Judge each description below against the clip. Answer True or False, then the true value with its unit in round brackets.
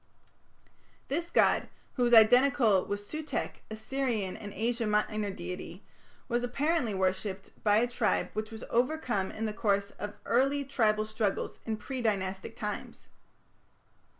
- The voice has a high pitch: True (220 Hz)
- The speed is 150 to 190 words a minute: False (140 wpm)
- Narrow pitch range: False (3.2 semitones)